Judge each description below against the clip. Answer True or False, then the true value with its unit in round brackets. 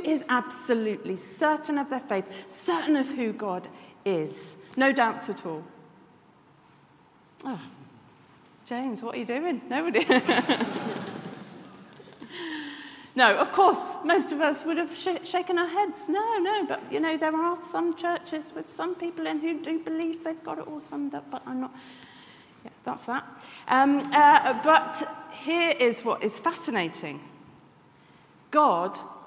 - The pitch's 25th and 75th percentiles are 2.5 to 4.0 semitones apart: False (5.2 semitones)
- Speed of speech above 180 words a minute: False (145 wpm)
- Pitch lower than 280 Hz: False (305 Hz)